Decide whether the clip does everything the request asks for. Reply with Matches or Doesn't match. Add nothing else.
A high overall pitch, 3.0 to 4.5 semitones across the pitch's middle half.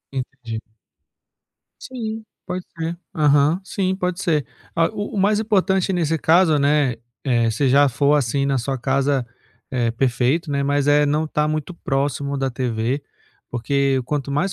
Doesn't match